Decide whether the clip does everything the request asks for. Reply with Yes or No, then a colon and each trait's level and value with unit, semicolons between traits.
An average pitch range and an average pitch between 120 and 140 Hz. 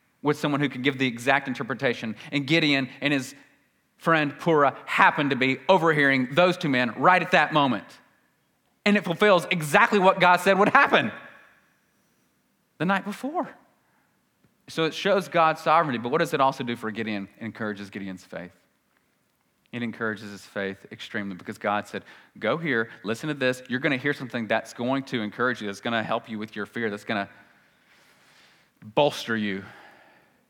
No: wide, 6.7 semitones; low, 135 Hz